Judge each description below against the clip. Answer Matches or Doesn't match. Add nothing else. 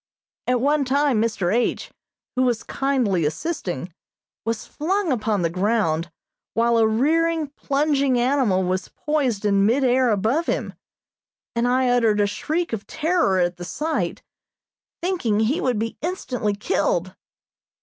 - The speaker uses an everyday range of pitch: Doesn't match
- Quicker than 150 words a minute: Doesn't match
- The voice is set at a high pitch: Matches